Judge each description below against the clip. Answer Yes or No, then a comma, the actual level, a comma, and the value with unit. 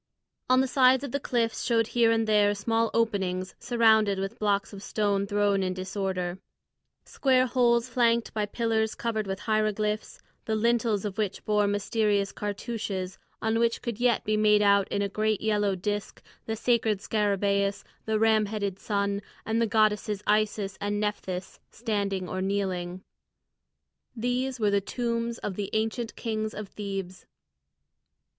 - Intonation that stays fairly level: Yes, narrow, 2.3 semitones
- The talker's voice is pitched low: No, high, 210 Hz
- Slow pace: No, average, 155 wpm